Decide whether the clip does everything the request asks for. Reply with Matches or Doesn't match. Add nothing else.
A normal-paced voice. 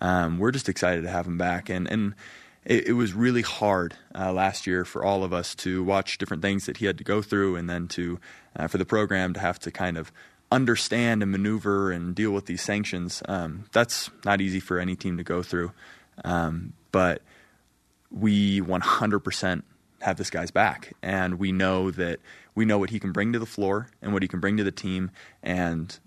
Doesn't match